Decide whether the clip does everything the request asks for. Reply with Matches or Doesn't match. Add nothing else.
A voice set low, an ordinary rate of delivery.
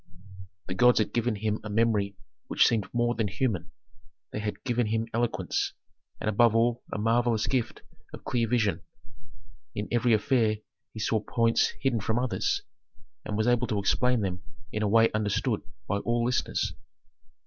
Matches